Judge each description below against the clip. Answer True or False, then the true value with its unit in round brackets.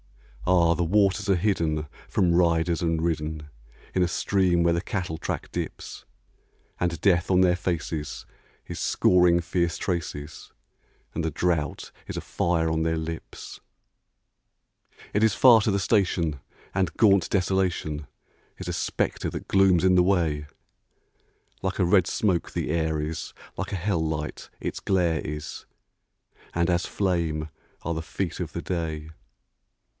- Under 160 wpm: True (150 wpm)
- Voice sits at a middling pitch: False (85 Hz)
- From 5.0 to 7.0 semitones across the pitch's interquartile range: False (2.5 semitones)